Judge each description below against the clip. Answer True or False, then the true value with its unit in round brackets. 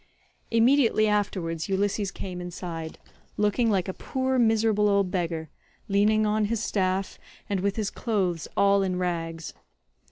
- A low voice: False (200 Hz)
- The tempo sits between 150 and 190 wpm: False (135 wpm)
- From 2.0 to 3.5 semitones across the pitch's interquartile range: True (3.1 semitones)